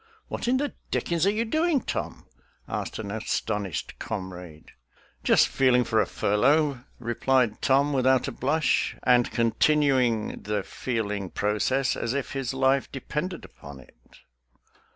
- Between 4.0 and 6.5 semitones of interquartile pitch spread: Yes, average, 5.0 semitones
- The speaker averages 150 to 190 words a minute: No, average, 140 wpm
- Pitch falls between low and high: No, low, 125 Hz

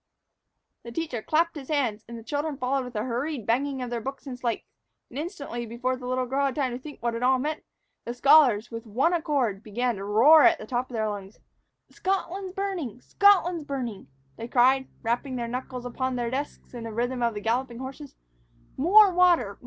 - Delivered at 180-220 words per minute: Yes, average, 200 wpm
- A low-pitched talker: No, very high, 255 Hz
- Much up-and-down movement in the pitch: No, average, 3.9 semitones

